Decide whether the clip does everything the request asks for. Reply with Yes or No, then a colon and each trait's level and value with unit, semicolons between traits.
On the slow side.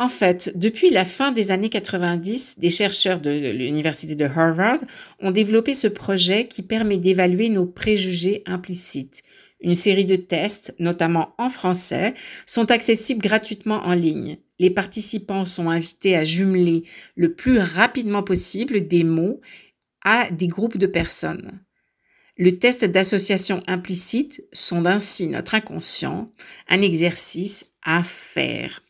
Yes: slow, 135 wpm